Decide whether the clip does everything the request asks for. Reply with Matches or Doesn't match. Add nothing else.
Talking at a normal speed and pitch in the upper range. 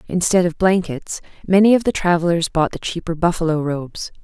Doesn't match